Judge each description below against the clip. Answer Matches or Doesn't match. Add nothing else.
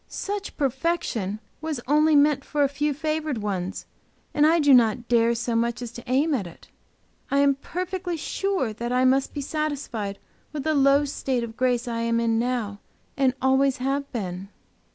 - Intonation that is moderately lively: Matches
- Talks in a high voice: Matches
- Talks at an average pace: Matches